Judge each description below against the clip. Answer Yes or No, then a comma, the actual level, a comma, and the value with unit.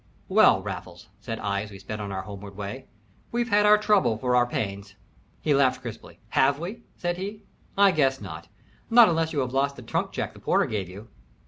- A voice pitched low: Yes, low, 130 Hz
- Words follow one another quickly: Yes, fast, 210 wpm